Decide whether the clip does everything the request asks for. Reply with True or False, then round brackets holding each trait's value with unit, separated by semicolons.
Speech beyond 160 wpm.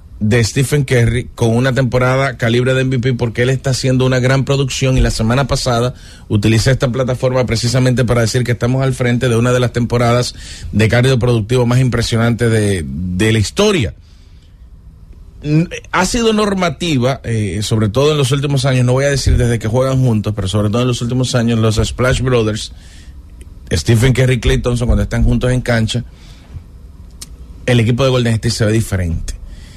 True (180 wpm)